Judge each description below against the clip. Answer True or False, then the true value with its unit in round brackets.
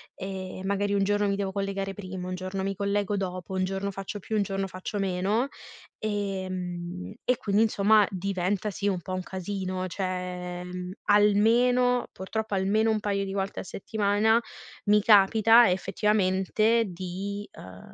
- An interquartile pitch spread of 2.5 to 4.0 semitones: False (1.8 semitones)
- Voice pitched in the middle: False (195 Hz)